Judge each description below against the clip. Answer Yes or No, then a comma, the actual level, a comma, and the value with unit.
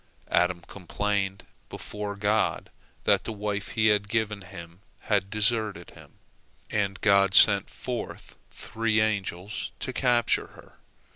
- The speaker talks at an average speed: No, slow, 125 wpm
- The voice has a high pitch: No, low, 105 Hz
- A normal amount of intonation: No, narrow, 1.8 semitones